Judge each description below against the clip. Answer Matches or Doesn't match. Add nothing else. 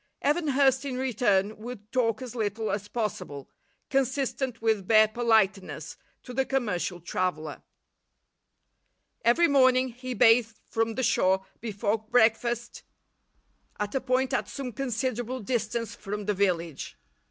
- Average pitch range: Matches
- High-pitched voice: Matches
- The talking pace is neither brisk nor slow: Doesn't match